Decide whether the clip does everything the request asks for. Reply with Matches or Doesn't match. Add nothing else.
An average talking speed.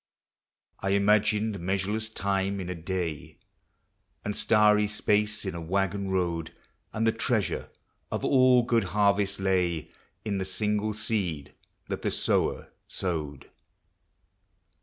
Doesn't match